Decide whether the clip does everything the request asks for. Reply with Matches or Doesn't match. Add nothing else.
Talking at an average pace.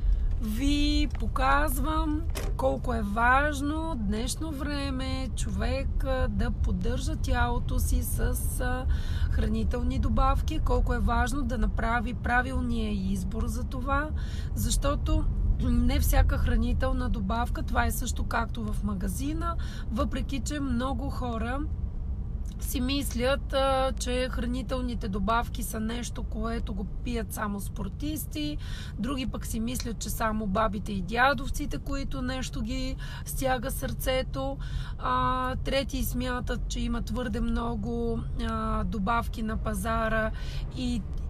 Doesn't match